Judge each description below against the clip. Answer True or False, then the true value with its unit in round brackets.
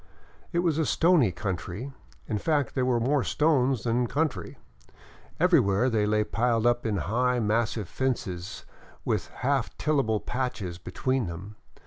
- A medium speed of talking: True (145 wpm)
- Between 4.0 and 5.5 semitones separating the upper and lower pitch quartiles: True (4.4 semitones)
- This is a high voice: False (120 Hz)